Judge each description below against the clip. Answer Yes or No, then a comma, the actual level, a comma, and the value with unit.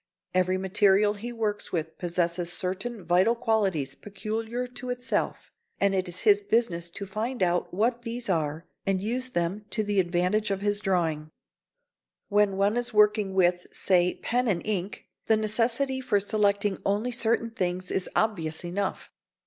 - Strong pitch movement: No, average, 3.8 semitones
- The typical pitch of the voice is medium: No, high, 200 Hz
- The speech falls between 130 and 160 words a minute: Yes, average, 155 wpm